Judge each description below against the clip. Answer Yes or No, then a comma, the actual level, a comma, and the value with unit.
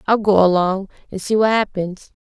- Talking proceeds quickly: No, average, 190 wpm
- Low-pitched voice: No, high, 195 Hz